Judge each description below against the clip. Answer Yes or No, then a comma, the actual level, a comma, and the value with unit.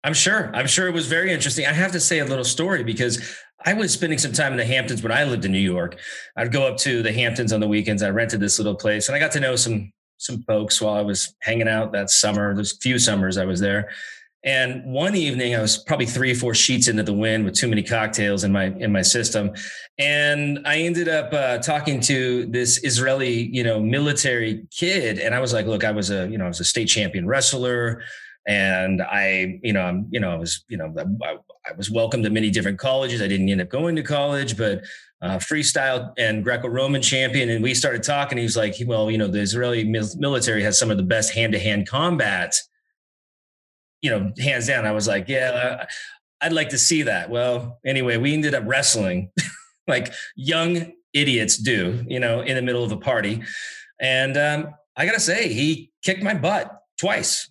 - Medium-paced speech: No, fast, 220 wpm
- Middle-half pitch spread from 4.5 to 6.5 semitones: Yes, average, 4.9 semitones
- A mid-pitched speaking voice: No, low, 120 Hz